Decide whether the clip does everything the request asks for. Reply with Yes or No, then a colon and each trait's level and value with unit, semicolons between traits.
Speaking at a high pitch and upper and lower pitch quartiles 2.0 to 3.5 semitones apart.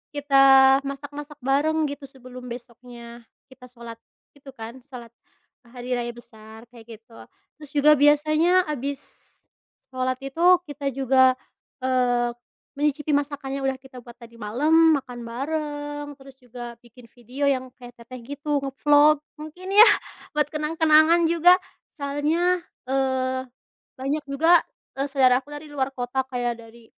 Yes: very high, 270 Hz; average, 3.0 semitones